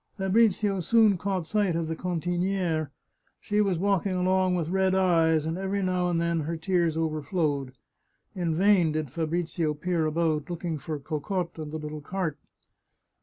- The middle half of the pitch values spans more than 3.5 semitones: No, average, 3.0 semitones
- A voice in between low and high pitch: Yes, medium, 170 Hz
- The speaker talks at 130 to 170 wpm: Yes, average, 165 wpm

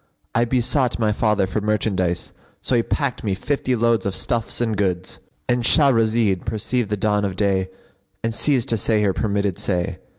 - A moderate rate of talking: Yes, average, 170 wpm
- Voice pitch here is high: No, low, 110 Hz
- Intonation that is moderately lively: Yes, average, 3.0 semitones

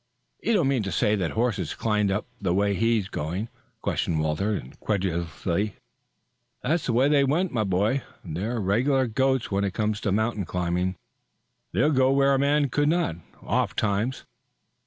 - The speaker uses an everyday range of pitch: No, wide, 5.7 semitones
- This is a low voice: Yes, low, 110 Hz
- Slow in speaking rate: No, average, 170 wpm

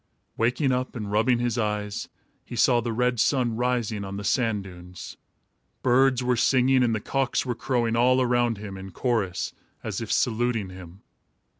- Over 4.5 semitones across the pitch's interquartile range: No, average, 3.1 semitones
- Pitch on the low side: Yes, low, 120 Hz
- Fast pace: No, average, 170 wpm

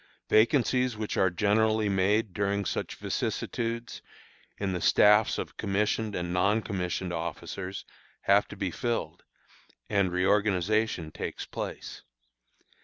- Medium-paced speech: No, slow, 115 wpm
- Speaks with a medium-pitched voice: No, low, 100 Hz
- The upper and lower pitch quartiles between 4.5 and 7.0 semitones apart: No, average, 2.8 semitones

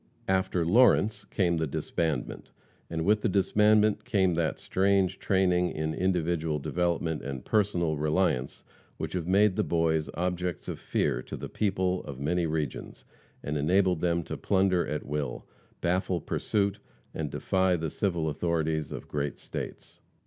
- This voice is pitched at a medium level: No, very low, 85 Hz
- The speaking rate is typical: Yes, average, 150 wpm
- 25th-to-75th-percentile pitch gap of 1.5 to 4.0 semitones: Yes, average, 3.2 semitones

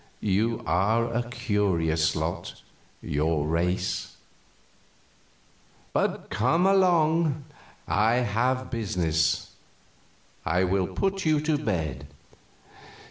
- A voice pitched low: Yes, low, 110 Hz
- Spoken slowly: Yes, slow, 85 wpm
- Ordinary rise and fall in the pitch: No, wide, 7.5 semitones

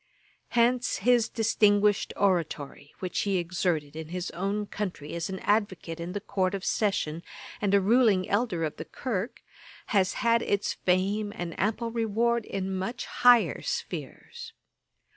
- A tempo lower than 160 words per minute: Yes, average, 145 wpm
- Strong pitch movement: No, average, 3.8 semitones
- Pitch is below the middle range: No, high, 200 Hz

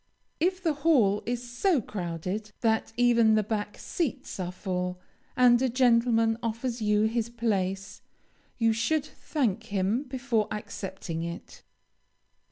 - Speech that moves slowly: Yes, slow, 130 wpm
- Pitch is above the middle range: Yes, high, 225 Hz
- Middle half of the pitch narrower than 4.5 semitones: Yes, average, 3.3 semitones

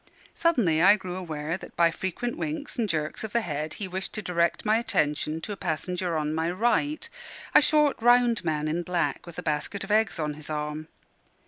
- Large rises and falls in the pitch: Yes, wide, 5.9 semitones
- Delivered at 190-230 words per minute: Yes, fast, 205 wpm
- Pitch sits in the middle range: Yes, medium, 180 Hz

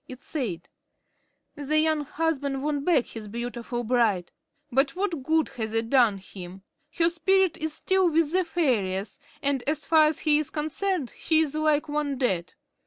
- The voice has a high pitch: Yes, very high, 290 Hz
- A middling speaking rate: Yes, average, 170 wpm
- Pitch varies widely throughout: No, average, 4.9 semitones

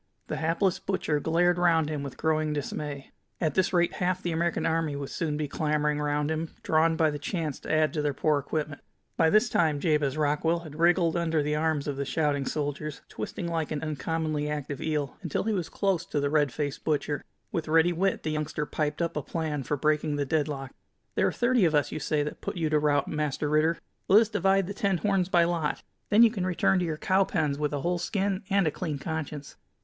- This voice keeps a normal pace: No, fast, 225 wpm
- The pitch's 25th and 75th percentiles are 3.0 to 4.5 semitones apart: No, narrow, 2.6 semitones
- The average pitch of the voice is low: No, medium, 155 Hz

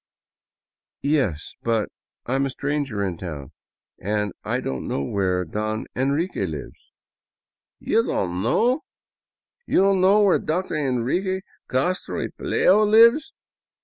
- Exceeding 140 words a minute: No, slow, 135 wpm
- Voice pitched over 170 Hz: No, low, 135 Hz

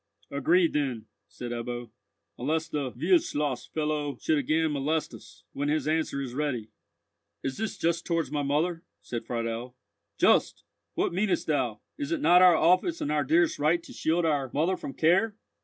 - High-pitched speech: No, medium, 150 Hz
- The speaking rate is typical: Yes, average, 170 wpm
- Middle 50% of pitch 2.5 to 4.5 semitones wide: Yes, average, 3.8 semitones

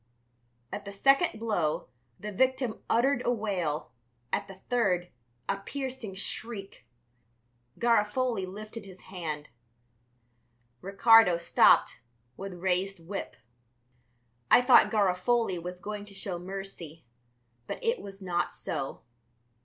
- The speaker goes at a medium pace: No, slow, 115 wpm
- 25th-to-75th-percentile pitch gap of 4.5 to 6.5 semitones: No, average, 4.1 semitones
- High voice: Yes, high, 195 Hz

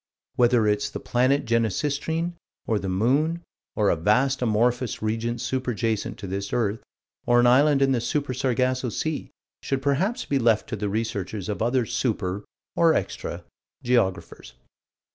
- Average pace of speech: Yes, average, 155 wpm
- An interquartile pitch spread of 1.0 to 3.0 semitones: No, average, 4.0 semitones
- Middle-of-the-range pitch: No, low, 120 Hz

